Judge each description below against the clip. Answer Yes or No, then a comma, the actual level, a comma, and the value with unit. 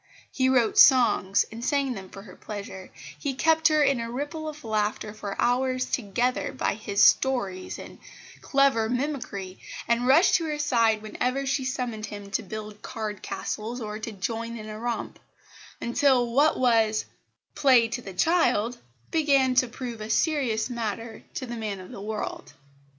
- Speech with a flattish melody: No, average, 3.7 semitones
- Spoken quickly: No, average, 165 wpm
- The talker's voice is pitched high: Yes, high, 235 Hz